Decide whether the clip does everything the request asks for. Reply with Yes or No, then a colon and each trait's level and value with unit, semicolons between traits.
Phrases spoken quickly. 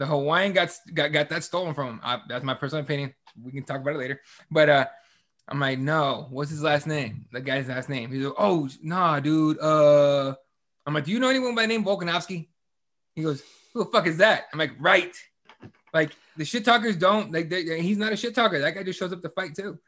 Yes: fast, 235 wpm